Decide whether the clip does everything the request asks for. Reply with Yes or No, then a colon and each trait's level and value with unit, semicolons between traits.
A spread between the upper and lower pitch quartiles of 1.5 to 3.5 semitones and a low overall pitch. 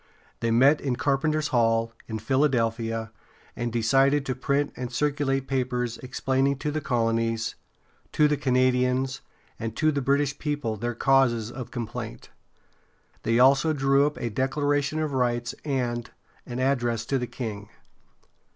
Yes: average, 2.9 semitones; low, 130 Hz